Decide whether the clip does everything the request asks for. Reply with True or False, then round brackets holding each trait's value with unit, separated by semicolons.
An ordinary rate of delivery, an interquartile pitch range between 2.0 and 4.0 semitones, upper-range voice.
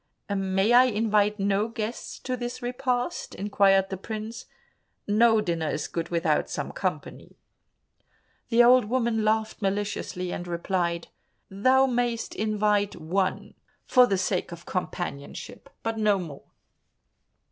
False (125 wpm; 3.7 semitones; 210 Hz)